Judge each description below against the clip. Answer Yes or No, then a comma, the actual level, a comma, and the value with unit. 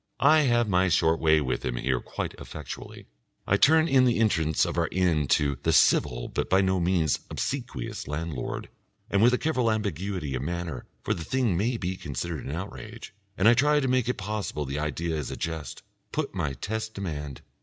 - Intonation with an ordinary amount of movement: No, wide, 6.7 semitones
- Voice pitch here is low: Yes, very low, 90 Hz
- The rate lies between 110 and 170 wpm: No, average, 195 wpm